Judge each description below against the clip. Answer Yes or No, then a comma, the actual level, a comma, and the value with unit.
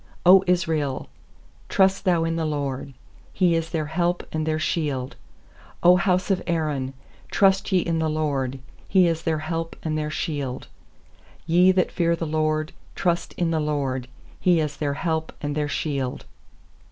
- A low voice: No, medium, 160 Hz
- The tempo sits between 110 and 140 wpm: No, average, 165 wpm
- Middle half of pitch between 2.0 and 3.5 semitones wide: Yes, average, 2.8 semitones